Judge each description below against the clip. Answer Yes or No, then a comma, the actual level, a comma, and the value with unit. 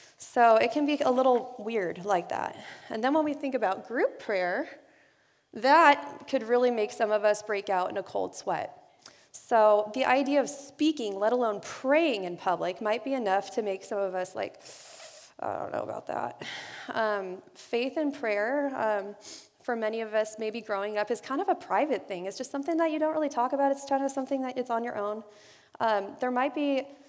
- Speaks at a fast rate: Yes, fast, 210 wpm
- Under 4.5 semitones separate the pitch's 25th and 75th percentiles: No, average, 4.9 semitones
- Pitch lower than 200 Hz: No, high, 245 Hz